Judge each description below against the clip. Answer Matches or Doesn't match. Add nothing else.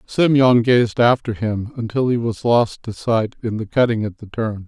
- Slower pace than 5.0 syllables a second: Matches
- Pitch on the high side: Doesn't match